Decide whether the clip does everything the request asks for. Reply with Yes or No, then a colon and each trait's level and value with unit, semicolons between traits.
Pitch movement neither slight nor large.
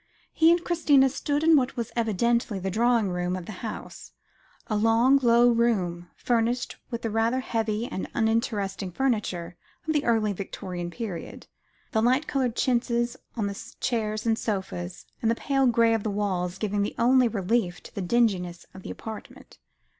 Yes: average, 3.6 semitones